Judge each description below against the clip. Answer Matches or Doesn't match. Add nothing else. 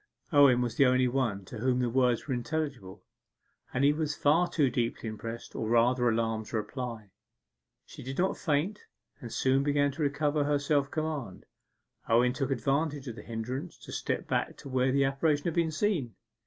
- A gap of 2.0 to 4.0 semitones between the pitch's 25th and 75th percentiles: Matches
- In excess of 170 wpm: Matches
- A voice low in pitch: Matches